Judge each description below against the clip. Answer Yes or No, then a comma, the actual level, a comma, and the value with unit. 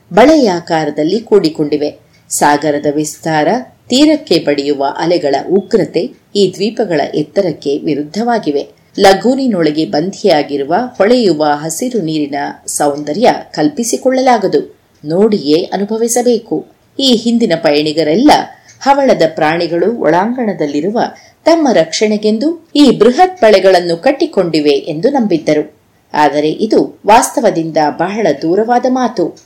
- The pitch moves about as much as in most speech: No, wide, 7.7 semitones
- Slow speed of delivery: No, average, 85 wpm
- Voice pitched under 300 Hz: Yes, medium, 185 Hz